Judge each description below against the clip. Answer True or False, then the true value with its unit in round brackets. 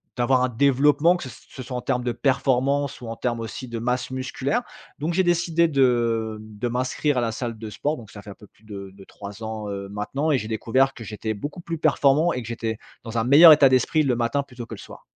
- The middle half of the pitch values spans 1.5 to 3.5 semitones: False (3.9 semitones)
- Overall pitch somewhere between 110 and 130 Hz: True (125 Hz)